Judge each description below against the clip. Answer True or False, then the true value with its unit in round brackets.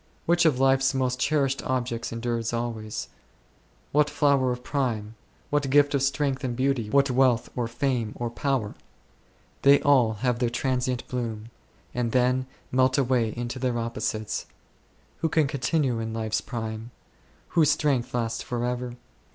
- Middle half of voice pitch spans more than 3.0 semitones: False (2.7 semitones)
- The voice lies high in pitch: False (125 Hz)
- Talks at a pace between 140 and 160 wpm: True (150 wpm)